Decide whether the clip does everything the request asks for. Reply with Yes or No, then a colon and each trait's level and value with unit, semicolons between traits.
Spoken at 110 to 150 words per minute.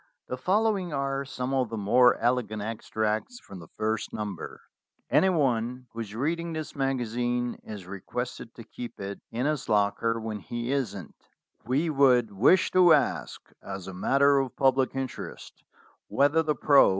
No: average, 160 wpm